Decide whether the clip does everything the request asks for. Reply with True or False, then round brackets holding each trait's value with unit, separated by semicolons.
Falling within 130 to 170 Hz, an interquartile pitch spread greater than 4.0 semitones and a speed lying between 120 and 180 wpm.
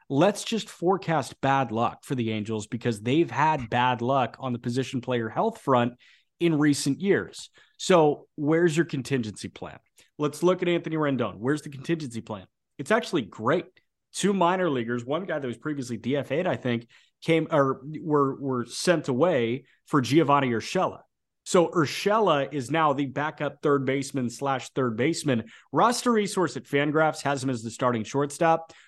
True (140 Hz; 4.5 semitones; 165 wpm)